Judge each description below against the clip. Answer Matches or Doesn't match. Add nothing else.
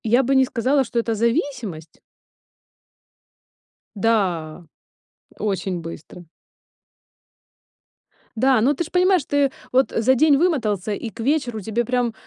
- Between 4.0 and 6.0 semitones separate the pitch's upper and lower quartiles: Matches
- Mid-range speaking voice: Doesn't match